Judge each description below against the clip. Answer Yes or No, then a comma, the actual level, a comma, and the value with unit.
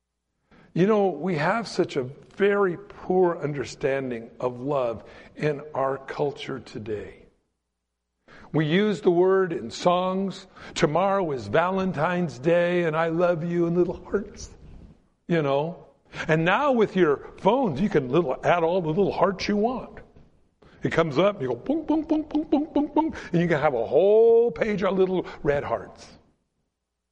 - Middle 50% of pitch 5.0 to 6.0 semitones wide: Yes, average, 5.3 semitones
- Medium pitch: Yes, medium, 175 Hz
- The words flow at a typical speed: Yes, average, 160 wpm